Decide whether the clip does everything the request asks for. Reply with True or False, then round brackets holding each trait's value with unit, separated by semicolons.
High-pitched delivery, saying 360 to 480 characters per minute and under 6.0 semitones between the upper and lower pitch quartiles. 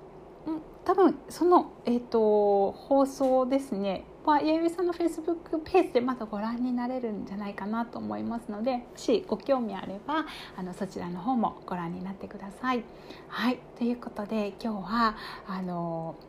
False (235 Hz; 335 characters per minute; 5.6 semitones)